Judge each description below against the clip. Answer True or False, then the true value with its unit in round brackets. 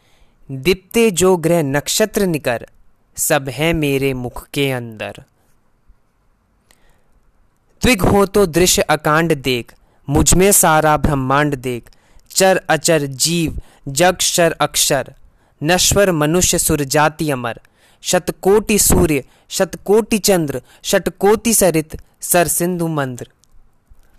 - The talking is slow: True (100 wpm)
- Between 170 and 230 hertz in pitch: False (160 Hz)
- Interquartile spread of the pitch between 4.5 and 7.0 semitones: True (5.1 semitones)